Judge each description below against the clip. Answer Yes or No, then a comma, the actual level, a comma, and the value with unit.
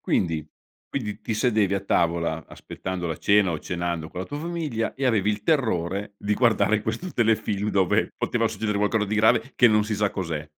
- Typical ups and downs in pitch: Yes, average, 3.9 semitones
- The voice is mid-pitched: No, low, 105 Hz